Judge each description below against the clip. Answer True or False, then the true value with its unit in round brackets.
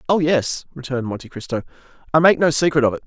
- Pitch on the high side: False (145 Hz)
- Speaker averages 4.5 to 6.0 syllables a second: False (7.1 syllables/s)